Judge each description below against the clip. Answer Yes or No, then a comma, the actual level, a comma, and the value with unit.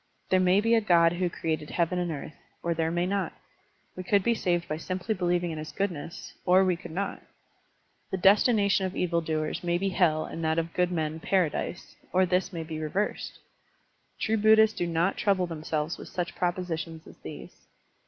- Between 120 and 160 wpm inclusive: No, average, 195 wpm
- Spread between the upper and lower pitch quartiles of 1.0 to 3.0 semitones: Yes, narrow, 2.6 semitones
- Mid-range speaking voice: Yes, medium, 175 Hz